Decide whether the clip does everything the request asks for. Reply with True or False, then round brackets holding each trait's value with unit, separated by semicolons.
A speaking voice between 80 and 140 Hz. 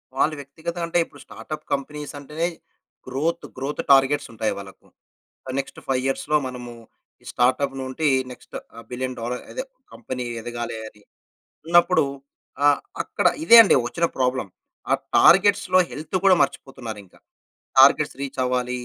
True (135 Hz)